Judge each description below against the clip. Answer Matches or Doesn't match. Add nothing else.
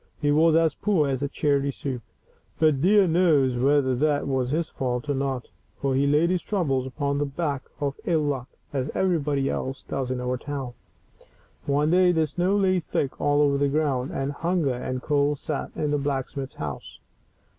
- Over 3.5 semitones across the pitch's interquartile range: Doesn't match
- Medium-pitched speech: Matches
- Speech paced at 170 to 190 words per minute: Matches